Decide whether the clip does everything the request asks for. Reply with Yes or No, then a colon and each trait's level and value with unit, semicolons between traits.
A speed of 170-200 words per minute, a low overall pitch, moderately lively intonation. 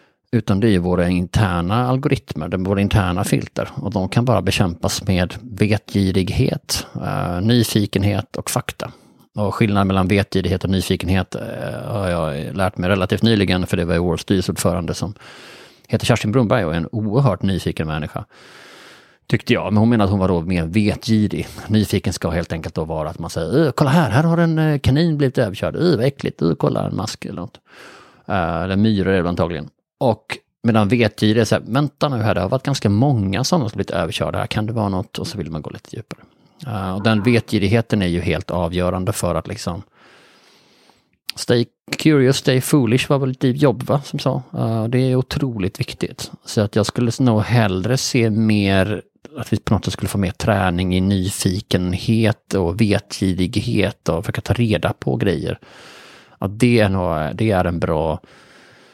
Yes: average, 190 wpm; low, 105 Hz; average, 4.2 semitones